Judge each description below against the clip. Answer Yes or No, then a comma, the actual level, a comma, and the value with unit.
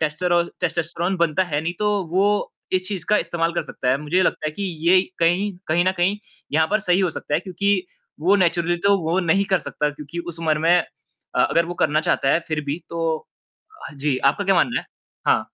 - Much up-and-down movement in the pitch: No, average, 3.0 semitones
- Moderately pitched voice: Yes, medium, 170 Hz